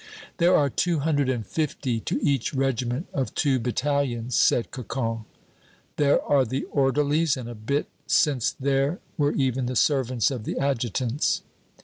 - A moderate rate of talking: Yes, average, 150 wpm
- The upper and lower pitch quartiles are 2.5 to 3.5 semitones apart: Yes, average, 2.8 semitones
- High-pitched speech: No, low, 135 Hz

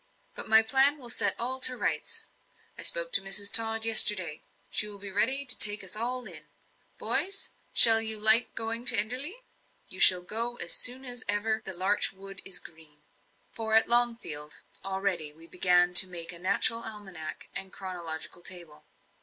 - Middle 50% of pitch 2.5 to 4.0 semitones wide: No, average, 4.6 semitones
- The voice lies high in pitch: Yes, high, 210 Hz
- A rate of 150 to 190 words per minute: Yes, average, 175 wpm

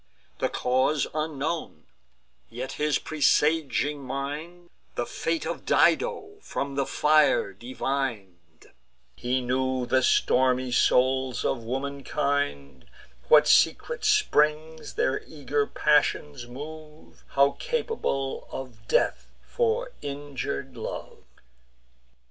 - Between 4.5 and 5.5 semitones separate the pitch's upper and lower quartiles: No, average, 3.2 semitones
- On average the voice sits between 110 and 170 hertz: Yes, medium, 140 Hz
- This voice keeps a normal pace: No, slow, 95 wpm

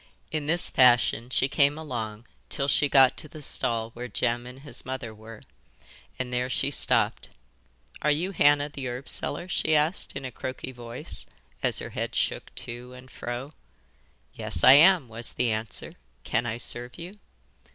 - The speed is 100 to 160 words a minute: No, average, 170 wpm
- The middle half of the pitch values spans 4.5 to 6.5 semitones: No, average, 3.3 semitones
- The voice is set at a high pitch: No, low, 130 Hz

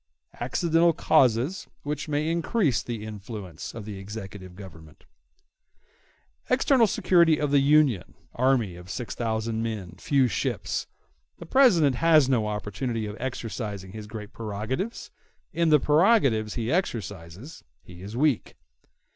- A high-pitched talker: No, low, 120 Hz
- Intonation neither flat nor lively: No, wide, 6.6 semitones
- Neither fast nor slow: No, slow, 120 wpm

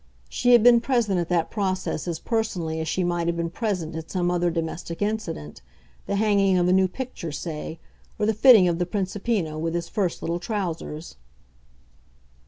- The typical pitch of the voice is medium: Yes, medium, 180 Hz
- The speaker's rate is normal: Yes, average, 185 wpm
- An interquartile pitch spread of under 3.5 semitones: No, average, 3.9 semitones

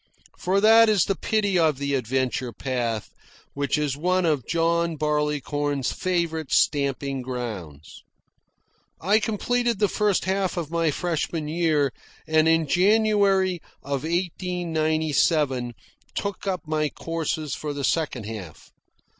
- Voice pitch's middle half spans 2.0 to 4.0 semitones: No, average, 4.5 semitones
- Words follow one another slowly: Yes, slow, 125 wpm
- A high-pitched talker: No, medium, 160 Hz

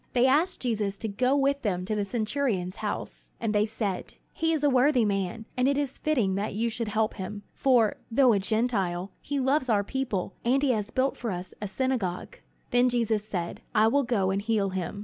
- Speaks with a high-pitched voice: Yes, high, 225 Hz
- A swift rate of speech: Yes, fast, 210 wpm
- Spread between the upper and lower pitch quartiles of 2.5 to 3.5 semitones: No, average, 4.6 semitones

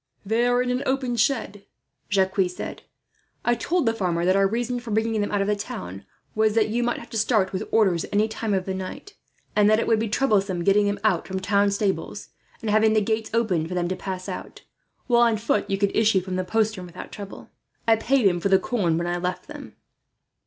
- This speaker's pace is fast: Yes, fast, 230 wpm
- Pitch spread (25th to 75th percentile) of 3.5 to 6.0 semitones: No, average, 3.1 semitones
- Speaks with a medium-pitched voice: No, high, 210 Hz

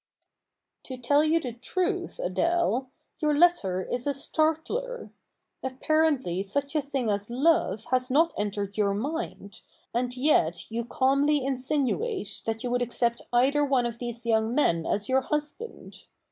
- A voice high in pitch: Yes, very high, 260 Hz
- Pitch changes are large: No, average, 4.5 semitones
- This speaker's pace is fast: No, average, 145 wpm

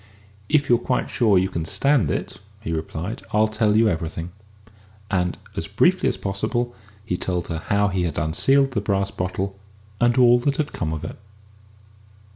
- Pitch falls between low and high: No, low, 100 Hz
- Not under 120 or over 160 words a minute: No, average, 175 wpm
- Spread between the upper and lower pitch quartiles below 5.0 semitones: No, wide, 5.4 semitones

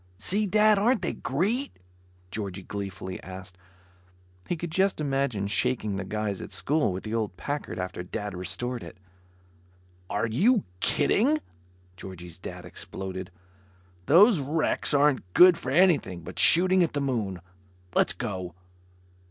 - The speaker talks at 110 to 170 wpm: Yes, slow, 135 wpm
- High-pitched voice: No, low, 125 Hz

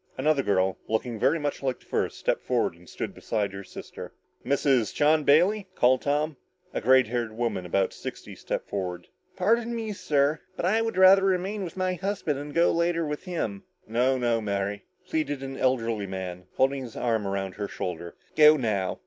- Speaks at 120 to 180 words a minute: No, average, 190 wpm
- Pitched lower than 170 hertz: Yes, low, 135 Hz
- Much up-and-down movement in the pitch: Yes, wide, 8.2 semitones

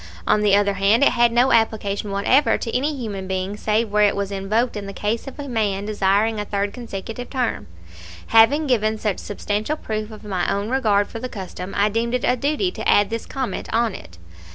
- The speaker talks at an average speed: No, fast, 215 wpm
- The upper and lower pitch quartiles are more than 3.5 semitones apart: No, average, 3.0 semitones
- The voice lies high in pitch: Yes, high, 215 Hz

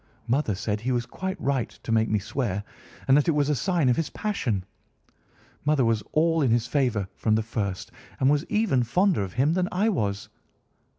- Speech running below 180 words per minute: No, average, 200 wpm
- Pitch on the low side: Yes, low, 130 Hz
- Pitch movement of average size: No, wide, 5.9 semitones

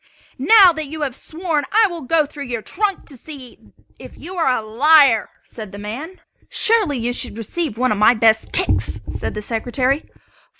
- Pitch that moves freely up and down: Yes, wide, 6.1 semitones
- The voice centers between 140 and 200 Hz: No, very high, 275 Hz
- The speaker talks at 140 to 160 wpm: No, average, 185 wpm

